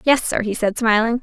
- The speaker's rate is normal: No, fast, 245 wpm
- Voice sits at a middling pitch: No, high, 230 Hz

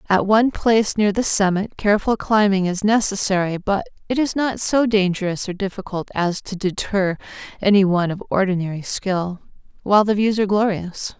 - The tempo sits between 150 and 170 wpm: Yes, average, 165 wpm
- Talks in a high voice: Yes, high, 200 Hz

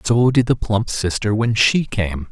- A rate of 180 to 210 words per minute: Yes, fast, 205 wpm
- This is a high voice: No, low, 110 Hz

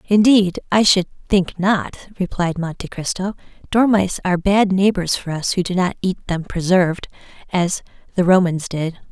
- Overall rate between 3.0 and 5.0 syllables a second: Yes, 4.9 syllables/s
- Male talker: No, female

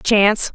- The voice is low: No, high, 210 Hz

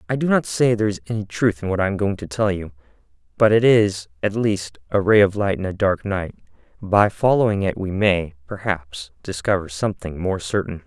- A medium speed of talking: No, fast, 215 wpm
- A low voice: Yes, low, 100 Hz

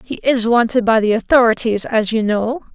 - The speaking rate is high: No, average, 195 wpm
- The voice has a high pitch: Yes, high, 230 Hz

